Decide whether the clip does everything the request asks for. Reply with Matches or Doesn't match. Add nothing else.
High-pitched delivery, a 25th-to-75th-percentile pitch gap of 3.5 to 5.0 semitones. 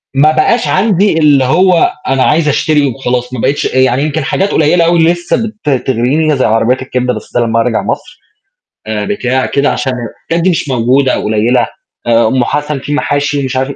Doesn't match